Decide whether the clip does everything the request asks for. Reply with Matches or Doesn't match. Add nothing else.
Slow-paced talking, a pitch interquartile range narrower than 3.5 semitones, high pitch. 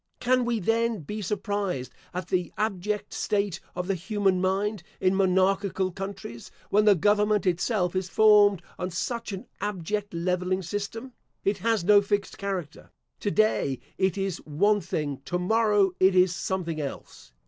Doesn't match